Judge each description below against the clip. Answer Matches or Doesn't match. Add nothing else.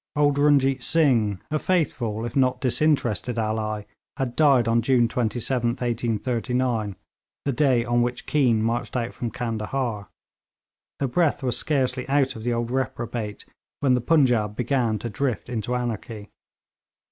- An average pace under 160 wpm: Matches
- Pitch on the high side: Doesn't match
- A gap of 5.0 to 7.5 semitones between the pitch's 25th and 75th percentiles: Doesn't match